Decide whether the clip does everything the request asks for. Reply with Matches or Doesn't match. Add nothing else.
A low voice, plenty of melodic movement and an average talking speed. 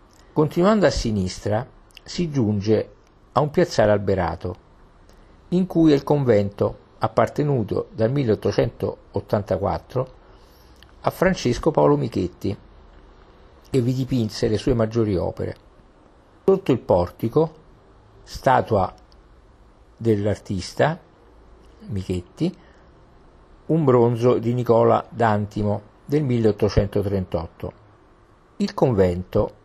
Doesn't match